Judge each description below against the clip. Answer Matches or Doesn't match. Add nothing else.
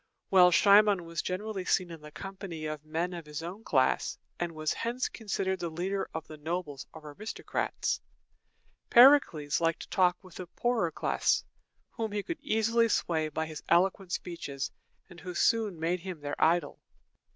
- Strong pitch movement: Doesn't match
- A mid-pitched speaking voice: Matches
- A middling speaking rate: Matches